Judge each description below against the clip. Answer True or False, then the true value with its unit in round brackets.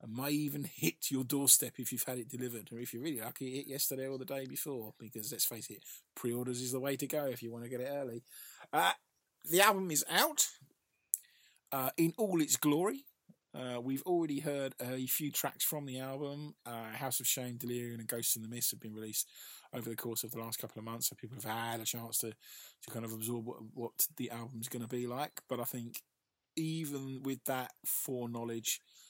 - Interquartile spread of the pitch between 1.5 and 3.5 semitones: True (2.8 semitones)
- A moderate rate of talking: False (225 wpm)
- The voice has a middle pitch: False (125 Hz)